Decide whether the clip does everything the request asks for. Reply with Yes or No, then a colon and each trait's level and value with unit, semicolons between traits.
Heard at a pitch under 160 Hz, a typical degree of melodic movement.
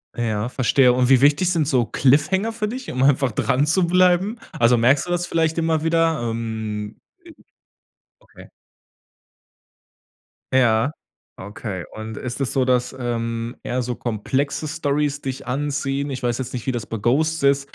Yes: low, 135 Hz; average, 4.6 semitones